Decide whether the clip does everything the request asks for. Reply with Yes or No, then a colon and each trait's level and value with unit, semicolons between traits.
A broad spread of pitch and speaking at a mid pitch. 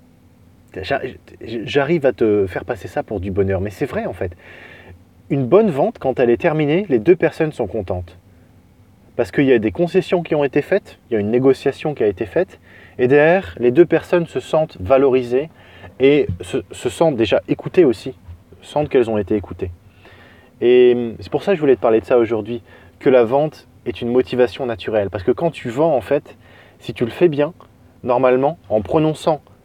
No: wide, 6.7 semitones; low, 120 Hz